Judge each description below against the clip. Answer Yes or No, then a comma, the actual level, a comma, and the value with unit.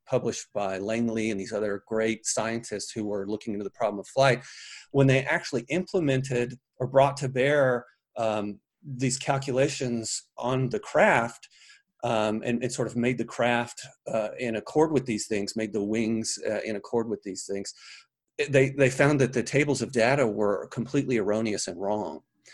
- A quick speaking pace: No, average, 175 wpm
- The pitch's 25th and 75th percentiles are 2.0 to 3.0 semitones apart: No, average, 3.6 semitones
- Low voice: Yes, low, 115 Hz